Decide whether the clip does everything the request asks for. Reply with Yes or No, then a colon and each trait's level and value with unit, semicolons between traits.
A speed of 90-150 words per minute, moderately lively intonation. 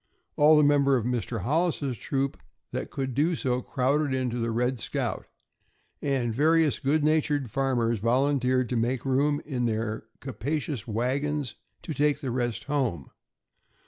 Yes: average, 145 wpm; average, 3.3 semitones